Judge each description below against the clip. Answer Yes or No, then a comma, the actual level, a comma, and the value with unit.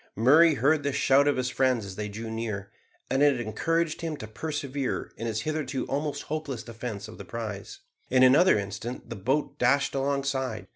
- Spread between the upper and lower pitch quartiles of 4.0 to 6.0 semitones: Yes, average, 4.3 semitones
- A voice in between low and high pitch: No, low, 130 Hz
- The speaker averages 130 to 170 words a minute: No, average, 185 wpm